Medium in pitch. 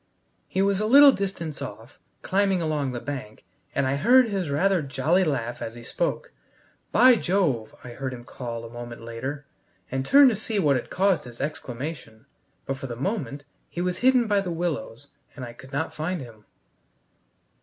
Yes: medium, 145 Hz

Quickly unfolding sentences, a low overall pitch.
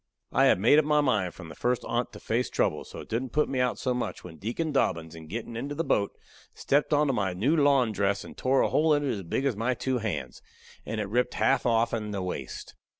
Yes: fast, 250 wpm; low, 120 Hz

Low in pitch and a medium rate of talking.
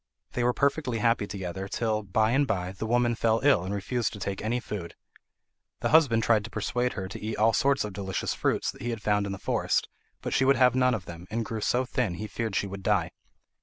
No: low, 110 Hz; fast, 240 wpm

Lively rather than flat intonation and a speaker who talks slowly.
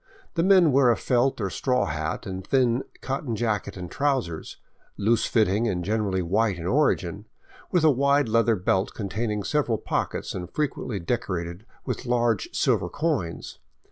No: wide, 5.8 semitones; average, 155 wpm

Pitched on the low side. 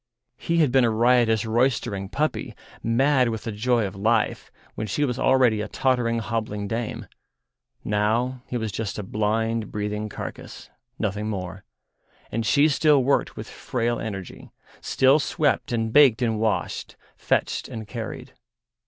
Yes: low, 115 Hz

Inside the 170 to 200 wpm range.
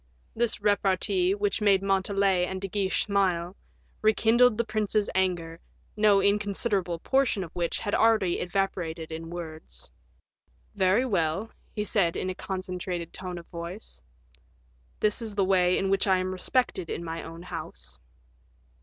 No: average, 145 wpm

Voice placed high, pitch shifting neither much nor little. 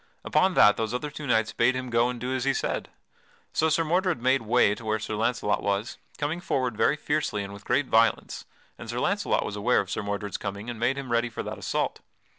No: low, 120 Hz; average, 4.1 semitones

